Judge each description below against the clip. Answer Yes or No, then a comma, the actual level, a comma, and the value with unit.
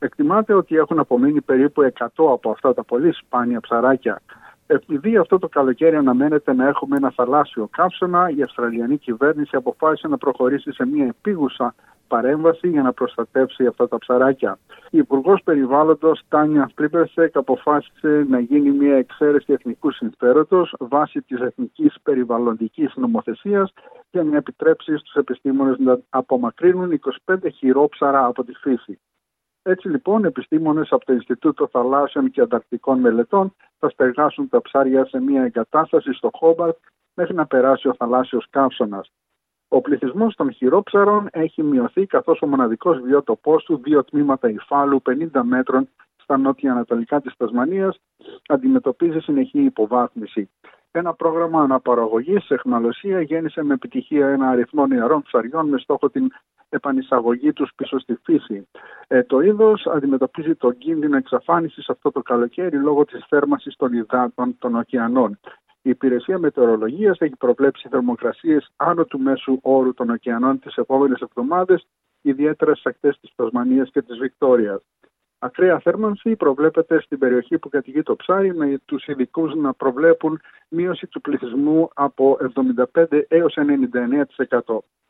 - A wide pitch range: No, average, 4.3 semitones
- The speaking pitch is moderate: Yes, medium, 145 Hz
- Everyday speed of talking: Yes, average, 140 wpm